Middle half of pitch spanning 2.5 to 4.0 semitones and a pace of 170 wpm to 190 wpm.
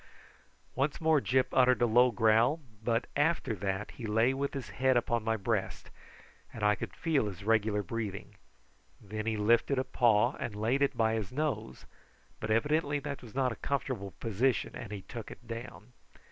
Yes: average, 3.5 semitones; average, 180 wpm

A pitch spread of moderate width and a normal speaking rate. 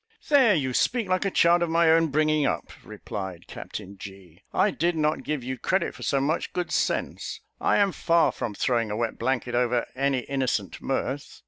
No: wide, 5.9 semitones; average, 195 wpm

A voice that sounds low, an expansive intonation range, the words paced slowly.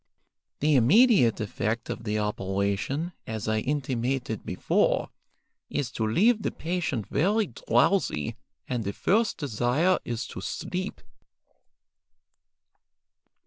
Yes: low, 125 Hz; wide, 8.1 semitones; slow, 105 wpm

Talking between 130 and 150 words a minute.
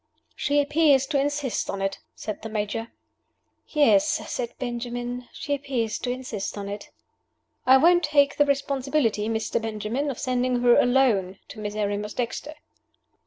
Yes: average, 145 wpm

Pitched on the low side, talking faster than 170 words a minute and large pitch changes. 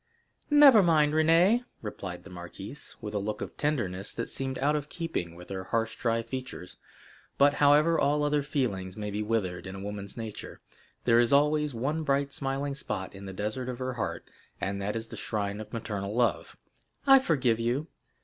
Yes: low, 120 Hz; average, 190 wpm; wide, 6.3 semitones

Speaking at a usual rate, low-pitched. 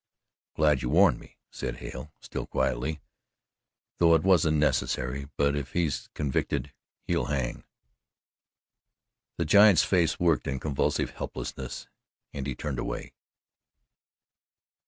No: slow, 120 wpm; very low, 75 Hz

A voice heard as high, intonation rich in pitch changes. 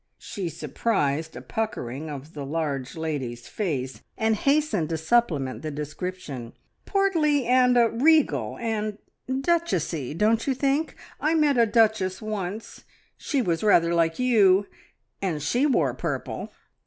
Yes: high, 200 Hz; wide, 8.0 semitones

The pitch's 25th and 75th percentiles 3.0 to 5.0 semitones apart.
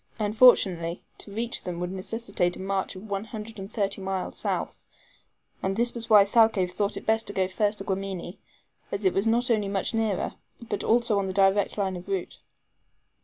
No: narrow, 2.6 semitones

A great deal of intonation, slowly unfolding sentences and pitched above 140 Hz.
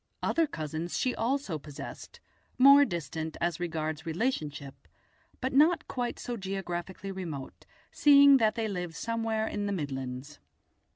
Yes: wide, 7.5 semitones; slow, 130 wpm; high, 190 Hz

